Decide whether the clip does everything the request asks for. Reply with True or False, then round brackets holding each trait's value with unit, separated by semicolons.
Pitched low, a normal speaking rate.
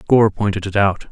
False (100 Hz; 215 wpm)